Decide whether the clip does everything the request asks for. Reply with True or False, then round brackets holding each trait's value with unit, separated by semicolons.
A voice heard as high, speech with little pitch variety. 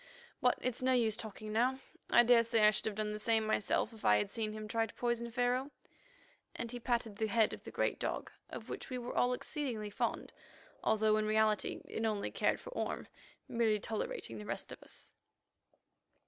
True (225 Hz; 2.1 semitones)